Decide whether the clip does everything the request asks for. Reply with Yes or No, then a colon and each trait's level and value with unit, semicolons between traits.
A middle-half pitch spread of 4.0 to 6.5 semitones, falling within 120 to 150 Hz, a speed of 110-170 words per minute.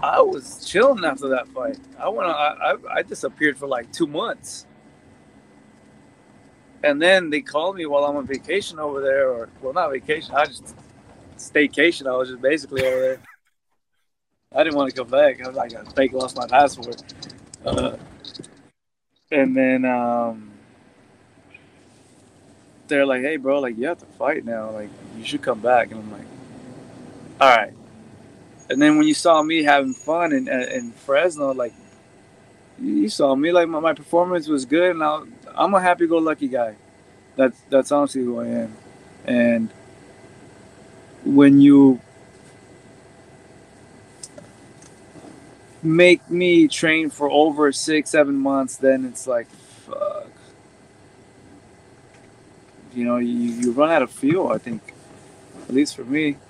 Yes: average, 4.7 semitones; low, 135 Hz; average, 150 wpm